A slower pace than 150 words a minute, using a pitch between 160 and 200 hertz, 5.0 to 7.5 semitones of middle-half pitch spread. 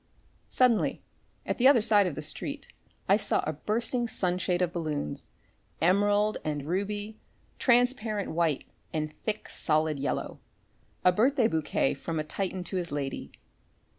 Yes: average, 140 wpm; medium, 185 Hz; wide, 5.5 semitones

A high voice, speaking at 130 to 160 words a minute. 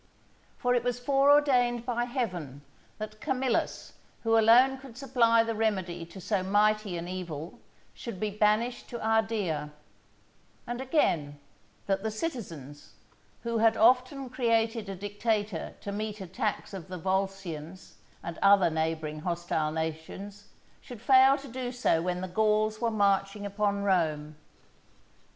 Yes: high, 210 Hz; average, 140 wpm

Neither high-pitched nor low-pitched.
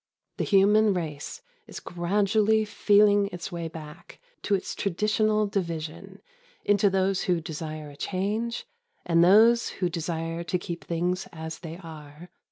Yes: medium, 180 Hz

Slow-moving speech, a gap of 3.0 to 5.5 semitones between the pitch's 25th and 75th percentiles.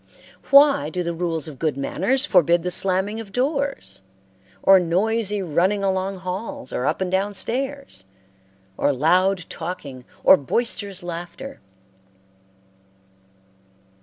Yes: slow, 120 wpm; average, 4.8 semitones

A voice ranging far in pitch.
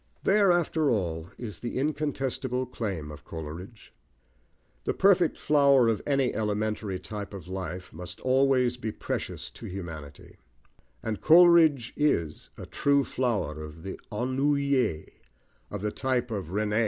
Yes: wide, 6.9 semitones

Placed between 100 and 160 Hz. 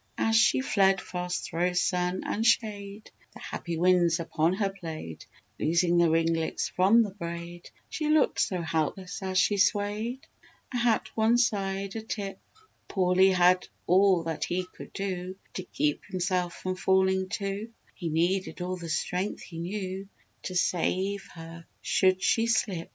No: medium, 185 Hz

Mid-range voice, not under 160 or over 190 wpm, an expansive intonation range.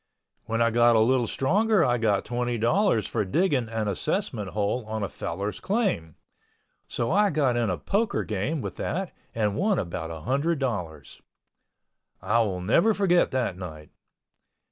No: low, 120 Hz; average, 165 wpm; wide, 8.1 semitones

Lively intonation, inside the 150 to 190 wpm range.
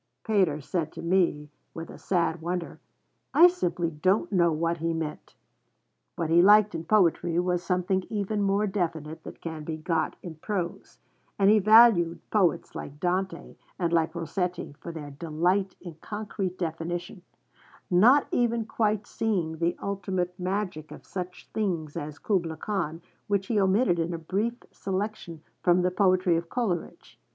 No: average, 3.3 semitones; average, 155 wpm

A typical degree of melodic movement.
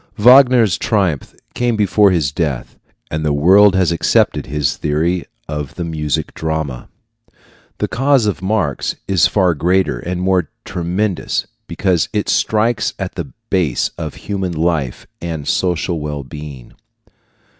Yes: average, 4.6 semitones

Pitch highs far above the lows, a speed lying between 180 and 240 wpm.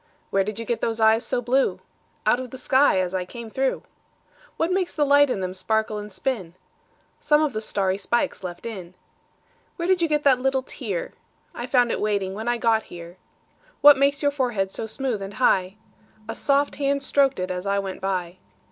Yes: wide, 6.0 semitones; average, 185 wpm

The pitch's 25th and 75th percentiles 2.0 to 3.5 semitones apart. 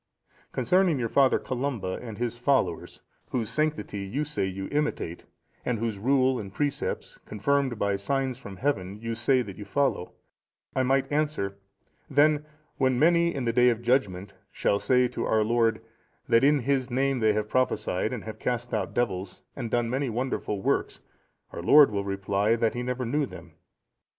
No: average, 4.6 semitones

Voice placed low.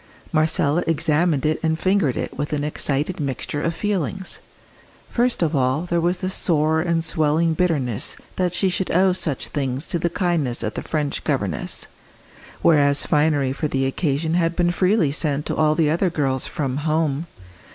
No: medium, 155 Hz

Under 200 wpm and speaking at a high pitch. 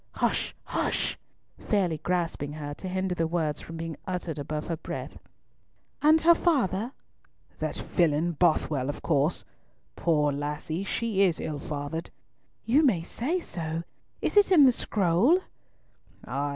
No: average, 140 wpm; medium, 170 Hz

